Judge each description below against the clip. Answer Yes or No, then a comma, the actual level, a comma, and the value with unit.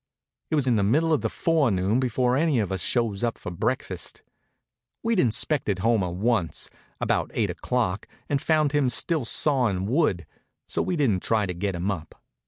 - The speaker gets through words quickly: No, average, 180 wpm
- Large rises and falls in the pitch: Yes, wide, 6.7 semitones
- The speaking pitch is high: No, low, 120 Hz